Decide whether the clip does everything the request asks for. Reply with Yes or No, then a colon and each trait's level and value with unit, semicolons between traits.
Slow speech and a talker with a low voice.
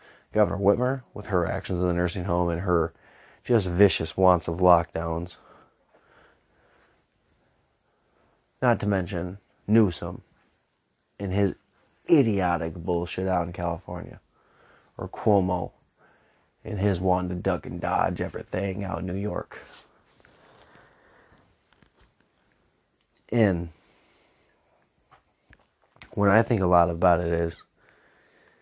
Yes: slow, 105 wpm; very low, 90 Hz